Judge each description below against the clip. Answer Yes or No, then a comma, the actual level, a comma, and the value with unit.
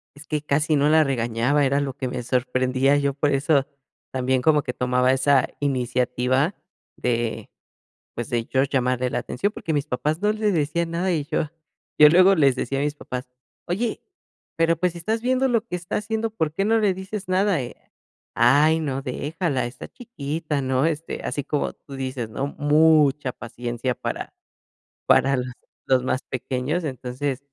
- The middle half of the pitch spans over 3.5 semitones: Yes, average, 4.3 semitones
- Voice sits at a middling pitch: Yes, medium, 145 Hz